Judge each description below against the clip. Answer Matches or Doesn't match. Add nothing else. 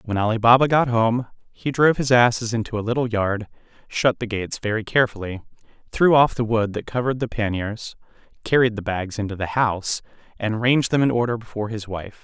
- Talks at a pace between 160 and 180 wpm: Doesn't match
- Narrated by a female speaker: Doesn't match